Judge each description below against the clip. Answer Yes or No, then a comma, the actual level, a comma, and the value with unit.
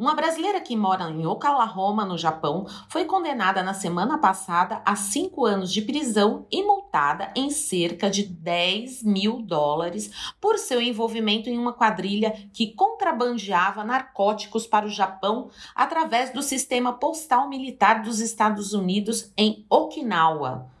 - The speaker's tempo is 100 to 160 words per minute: Yes, average, 140 wpm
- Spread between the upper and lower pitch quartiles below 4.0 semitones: No, average, 4.8 semitones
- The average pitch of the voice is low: No, high, 220 Hz